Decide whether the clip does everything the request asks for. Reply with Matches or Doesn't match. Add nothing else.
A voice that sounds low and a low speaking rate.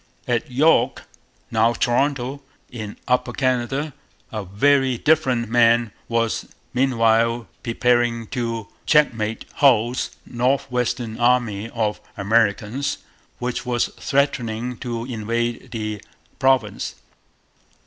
Matches